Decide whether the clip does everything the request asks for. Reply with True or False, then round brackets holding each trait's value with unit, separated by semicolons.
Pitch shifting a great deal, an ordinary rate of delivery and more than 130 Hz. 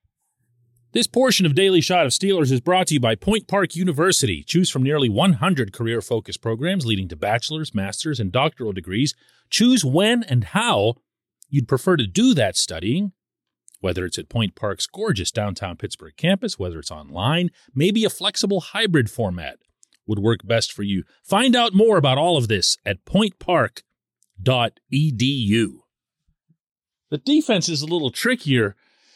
True (8.9 semitones; 155 wpm; 140 Hz)